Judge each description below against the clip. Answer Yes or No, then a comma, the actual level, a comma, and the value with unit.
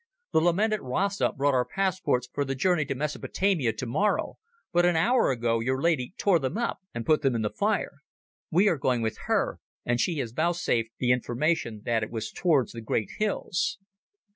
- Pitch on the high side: No, medium, 140 Hz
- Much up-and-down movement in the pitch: Yes, wide, 6.6 semitones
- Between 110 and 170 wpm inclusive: No, average, 185 wpm